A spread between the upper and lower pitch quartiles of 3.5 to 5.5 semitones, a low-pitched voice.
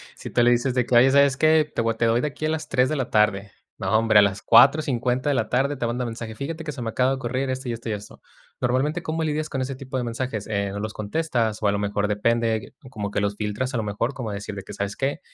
Yes: average, 4.0 semitones; low, 120 Hz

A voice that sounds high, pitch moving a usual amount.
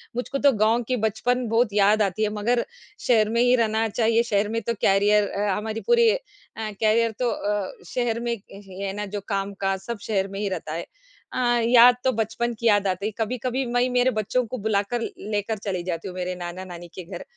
Yes: high, 215 Hz; average, 3.1 semitones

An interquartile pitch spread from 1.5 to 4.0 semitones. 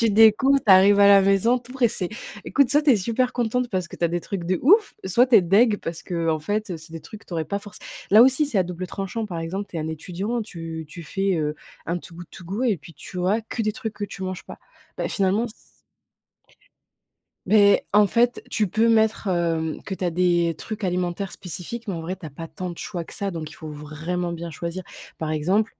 No: average, 4.4 semitones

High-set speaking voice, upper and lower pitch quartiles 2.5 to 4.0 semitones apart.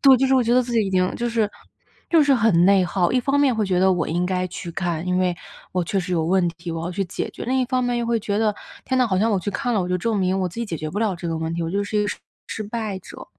No: high, 195 Hz; average, 4.6 semitones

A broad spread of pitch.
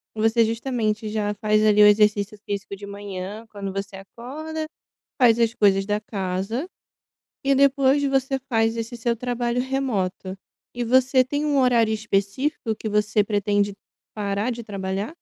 No: average, 3.5 semitones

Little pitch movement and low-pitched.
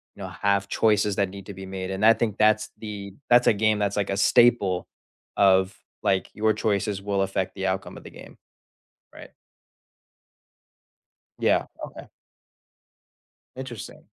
Yes: narrow, 1.9 semitones; low, 100 Hz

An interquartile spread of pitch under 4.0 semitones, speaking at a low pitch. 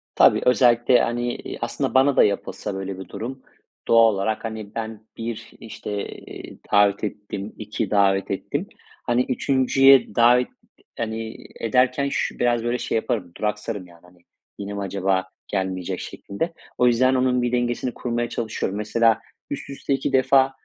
Yes: average, 3.4 semitones; low, 115 Hz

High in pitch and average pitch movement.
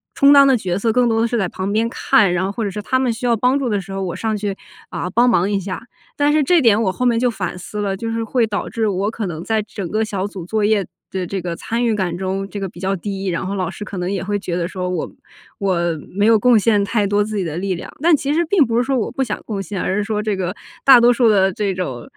Yes: high, 205 Hz; average, 3.4 semitones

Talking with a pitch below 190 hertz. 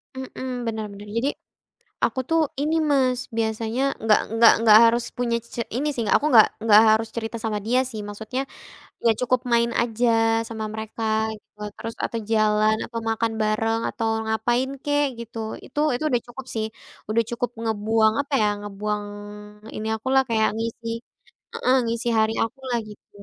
No: high, 230 Hz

